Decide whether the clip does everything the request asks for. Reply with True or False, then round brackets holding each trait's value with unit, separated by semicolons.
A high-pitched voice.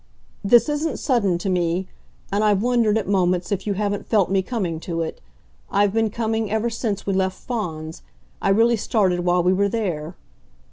True (200 Hz)